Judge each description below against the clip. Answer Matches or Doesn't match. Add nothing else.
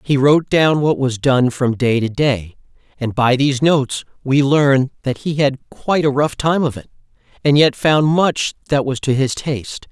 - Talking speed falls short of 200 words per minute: Doesn't match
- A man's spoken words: Matches